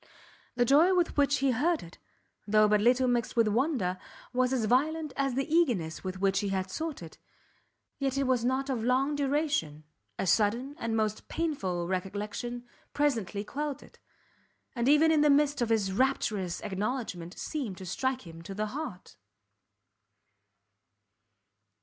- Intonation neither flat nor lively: No, wide, 5.9 semitones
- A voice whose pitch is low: No, high, 245 Hz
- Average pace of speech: Yes, average, 155 wpm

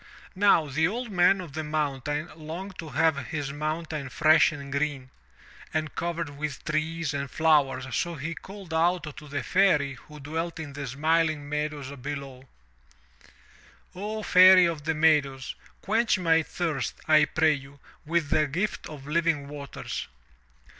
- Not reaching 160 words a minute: Yes, average, 150 wpm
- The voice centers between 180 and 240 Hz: No, medium, 155 Hz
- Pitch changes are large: No, average, 2.7 semitones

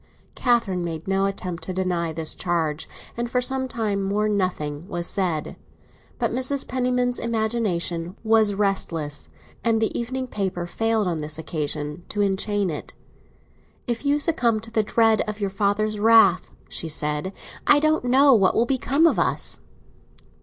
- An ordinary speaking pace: Yes, average, 155 wpm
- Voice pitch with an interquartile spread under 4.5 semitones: No, average, 5.2 semitones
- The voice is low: No, high, 205 Hz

